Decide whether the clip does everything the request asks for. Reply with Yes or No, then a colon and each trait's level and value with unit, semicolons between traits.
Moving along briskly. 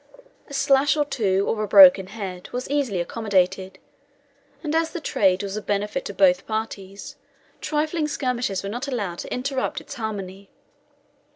No: average, 160 wpm